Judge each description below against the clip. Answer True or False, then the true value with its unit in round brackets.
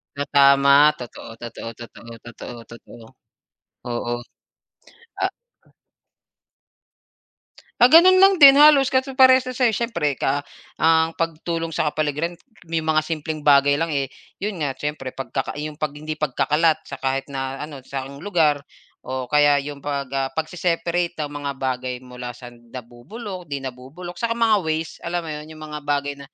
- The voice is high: False (150 Hz)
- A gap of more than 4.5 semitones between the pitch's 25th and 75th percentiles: False (3.8 semitones)